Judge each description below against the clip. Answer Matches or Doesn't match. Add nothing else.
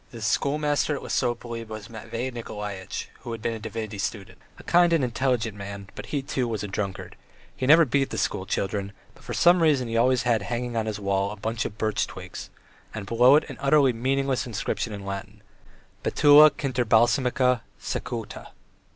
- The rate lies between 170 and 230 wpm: Matches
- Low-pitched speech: Matches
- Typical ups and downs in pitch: Matches